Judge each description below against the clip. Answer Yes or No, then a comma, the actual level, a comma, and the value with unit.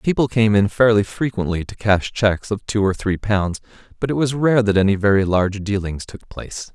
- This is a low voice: Yes, low, 105 Hz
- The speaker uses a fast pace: Yes, fast, 215 wpm